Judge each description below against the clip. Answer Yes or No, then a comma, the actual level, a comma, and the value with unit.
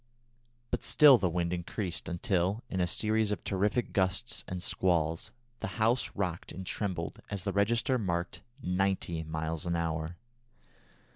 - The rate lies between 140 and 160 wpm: Yes, average, 145 wpm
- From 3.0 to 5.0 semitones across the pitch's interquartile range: Yes, average, 3.4 semitones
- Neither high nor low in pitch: No, very low, 95 Hz